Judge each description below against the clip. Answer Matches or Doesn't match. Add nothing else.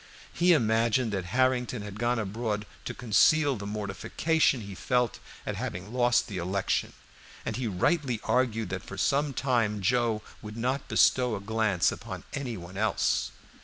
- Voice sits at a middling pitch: Doesn't match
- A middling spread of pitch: Matches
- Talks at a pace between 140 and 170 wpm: Matches